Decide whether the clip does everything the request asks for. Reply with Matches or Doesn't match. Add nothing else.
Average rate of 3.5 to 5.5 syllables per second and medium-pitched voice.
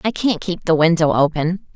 Matches